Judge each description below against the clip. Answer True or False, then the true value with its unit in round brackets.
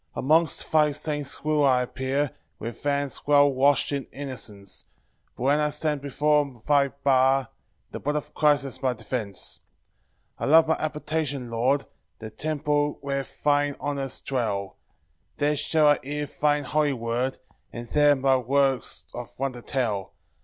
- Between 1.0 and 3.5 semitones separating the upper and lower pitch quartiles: True (2.4 semitones)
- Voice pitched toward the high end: False (140 Hz)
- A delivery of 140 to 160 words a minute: True (155 wpm)